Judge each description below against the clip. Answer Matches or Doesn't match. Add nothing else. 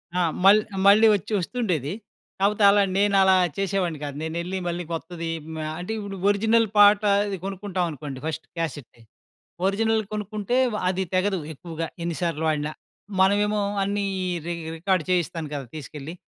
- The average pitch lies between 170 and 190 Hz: Matches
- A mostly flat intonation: Doesn't match